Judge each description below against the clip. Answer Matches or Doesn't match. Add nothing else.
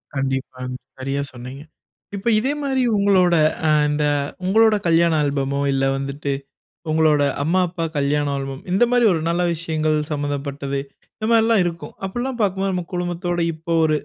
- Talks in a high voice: Doesn't match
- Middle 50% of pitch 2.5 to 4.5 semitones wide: Doesn't match